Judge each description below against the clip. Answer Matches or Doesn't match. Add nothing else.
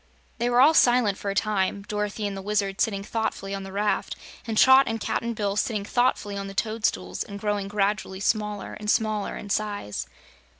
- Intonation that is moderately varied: Doesn't match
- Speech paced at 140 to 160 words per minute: Doesn't match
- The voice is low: Doesn't match